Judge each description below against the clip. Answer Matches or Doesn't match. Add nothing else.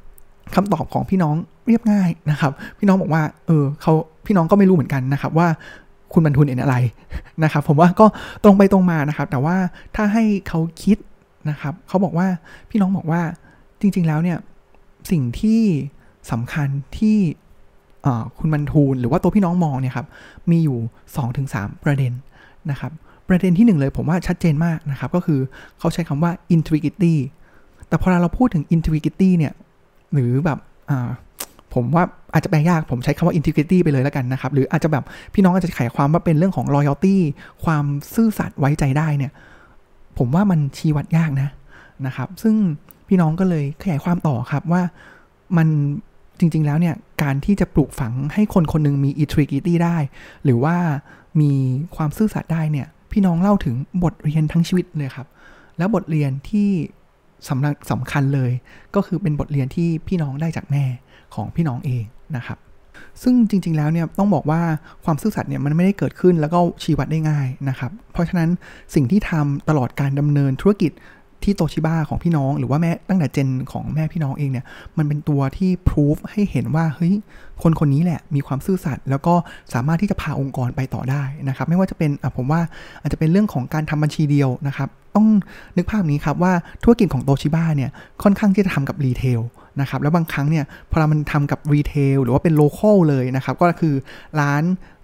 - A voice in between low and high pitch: Matches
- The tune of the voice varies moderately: Matches